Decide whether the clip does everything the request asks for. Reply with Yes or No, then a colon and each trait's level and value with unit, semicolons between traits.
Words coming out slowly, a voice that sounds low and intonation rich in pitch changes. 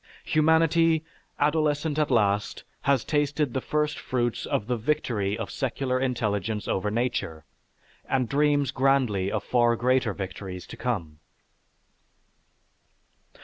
Yes: slow, 115 wpm; low, 125 Hz; wide, 5.8 semitones